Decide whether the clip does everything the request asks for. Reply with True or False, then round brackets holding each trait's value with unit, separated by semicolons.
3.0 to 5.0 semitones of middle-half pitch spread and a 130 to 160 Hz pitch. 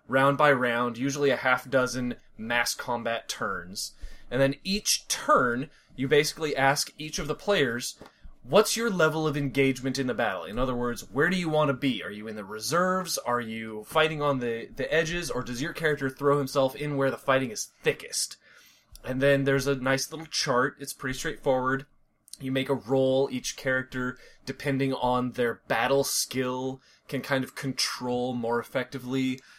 False (2.4 semitones; 135 Hz)